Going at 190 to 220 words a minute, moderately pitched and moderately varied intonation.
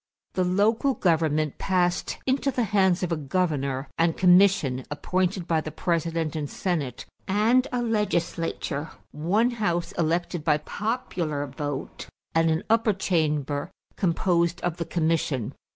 No: slow, 135 wpm; medium, 170 Hz; average, 3.8 semitones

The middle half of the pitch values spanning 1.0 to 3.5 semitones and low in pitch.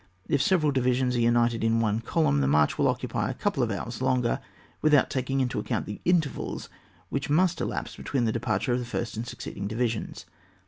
Yes: average, 3.2 semitones; low, 120 Hz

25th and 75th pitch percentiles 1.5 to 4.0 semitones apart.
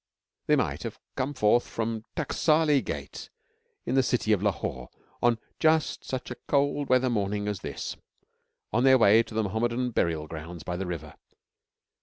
No: average, 4.8 semitones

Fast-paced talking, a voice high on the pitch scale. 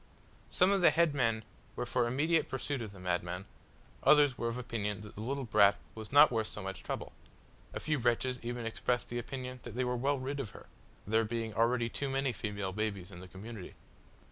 No: fast, 210 wpm; low, 120 Hz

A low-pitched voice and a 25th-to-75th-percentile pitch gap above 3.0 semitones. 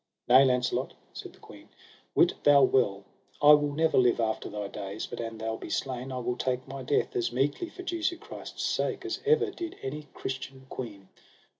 Yes: low, 130 Hz; average, 3.8 semitones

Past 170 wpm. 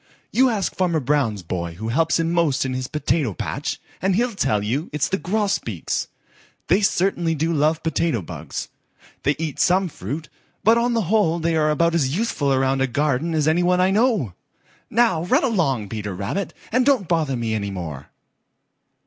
Yes: average, 185 wpm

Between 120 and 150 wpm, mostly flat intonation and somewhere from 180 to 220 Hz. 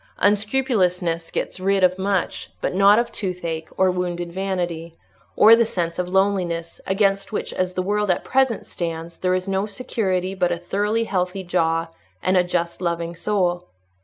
No: average, 165 wpm; narrow, 2.3 semitones; medium, 185 Hz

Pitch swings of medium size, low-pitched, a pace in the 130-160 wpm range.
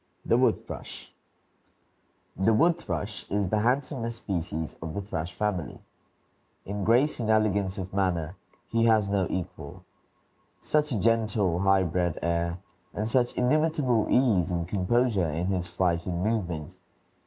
Yes: average, 4.4 semitones; low, 100 Hz; average, 140 wpm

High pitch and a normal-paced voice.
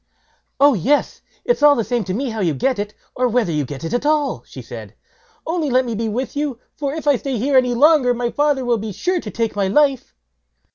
No: very high, 250 Hz; fast, 240 wpm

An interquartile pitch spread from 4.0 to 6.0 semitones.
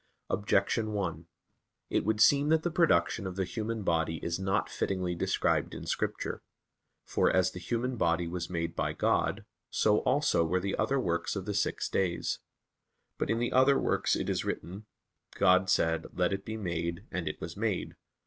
Yes: average, 4.3 semitones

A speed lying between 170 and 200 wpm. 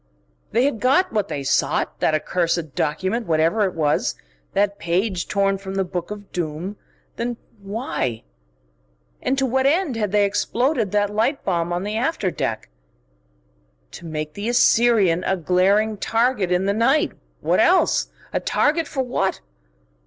No: average, 155 wpm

